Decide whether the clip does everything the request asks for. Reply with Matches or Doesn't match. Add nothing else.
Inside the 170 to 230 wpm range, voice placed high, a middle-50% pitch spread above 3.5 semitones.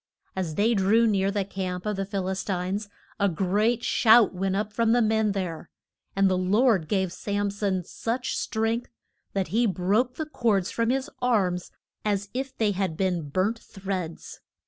Doesn't match